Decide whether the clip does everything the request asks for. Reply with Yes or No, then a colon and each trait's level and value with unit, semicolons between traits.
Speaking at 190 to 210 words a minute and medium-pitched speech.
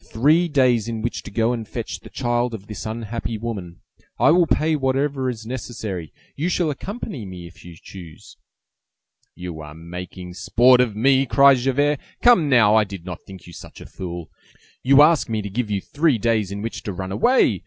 No: average, 195 wpm; low, 115 Hz